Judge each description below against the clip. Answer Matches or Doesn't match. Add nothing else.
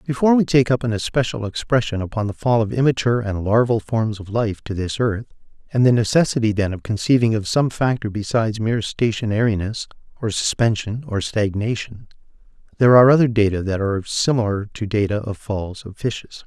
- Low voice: Matches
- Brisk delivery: Doesn't match